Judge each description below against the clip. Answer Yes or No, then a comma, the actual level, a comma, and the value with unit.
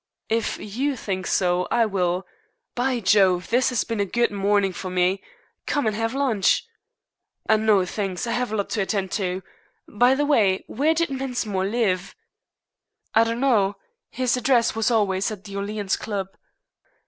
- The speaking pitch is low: No, high, 215 Hz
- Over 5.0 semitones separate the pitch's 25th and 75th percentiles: No, average, 3.8 semitones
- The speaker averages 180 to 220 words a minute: No, average, 165 wpm